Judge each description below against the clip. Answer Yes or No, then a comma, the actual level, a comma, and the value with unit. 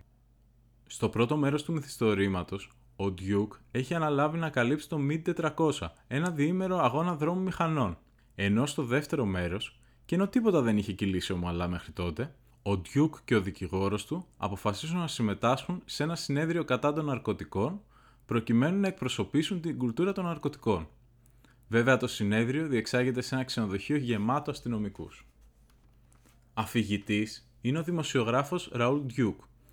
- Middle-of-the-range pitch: No, low, 120 Hz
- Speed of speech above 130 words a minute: Yes, average, 140 wpm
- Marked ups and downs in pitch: Yes, wide, 5.8 semitones